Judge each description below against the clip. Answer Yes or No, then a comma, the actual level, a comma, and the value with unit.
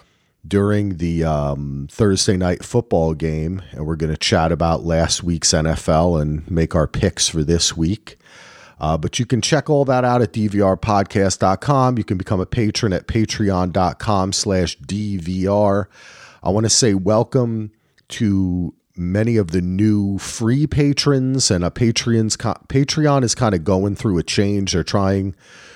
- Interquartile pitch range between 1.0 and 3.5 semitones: No, average, 4.4 semitones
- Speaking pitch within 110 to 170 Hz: No, low, 100 Hz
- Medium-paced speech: Yes, average, 155 wpm